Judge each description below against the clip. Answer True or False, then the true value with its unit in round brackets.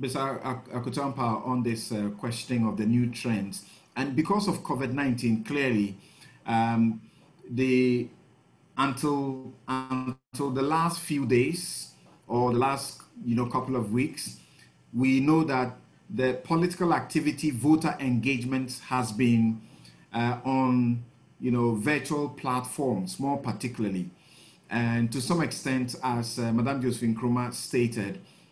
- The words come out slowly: True (125 wpm)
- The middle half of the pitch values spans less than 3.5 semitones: True (2.7 semitones)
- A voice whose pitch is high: False (125 Hz)